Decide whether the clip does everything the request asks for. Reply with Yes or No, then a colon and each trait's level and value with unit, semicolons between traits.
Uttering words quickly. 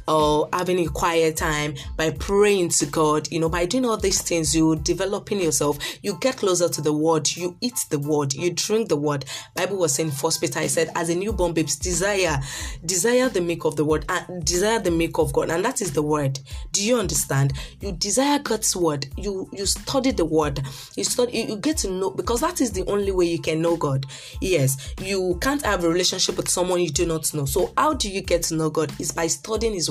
Yes: fast, 235 wpm